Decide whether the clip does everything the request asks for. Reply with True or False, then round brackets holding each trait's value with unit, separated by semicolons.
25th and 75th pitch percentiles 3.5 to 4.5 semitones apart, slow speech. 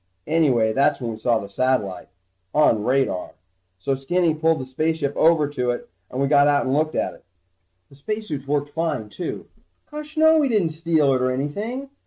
False (4.2 semitones; 190 wpm)